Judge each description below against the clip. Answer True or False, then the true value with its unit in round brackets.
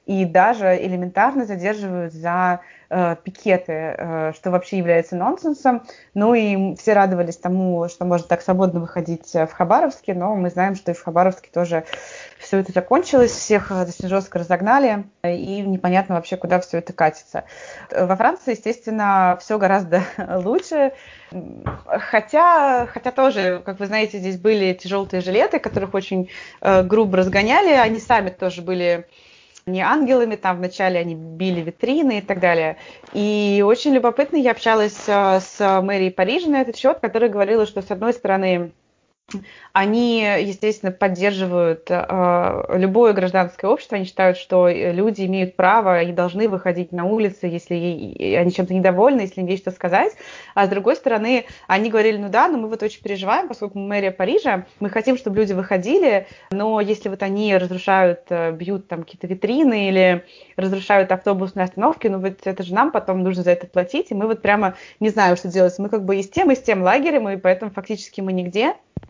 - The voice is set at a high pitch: True (195 Hz)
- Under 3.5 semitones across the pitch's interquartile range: True (3.0 semitones)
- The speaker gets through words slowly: False (170 wpm)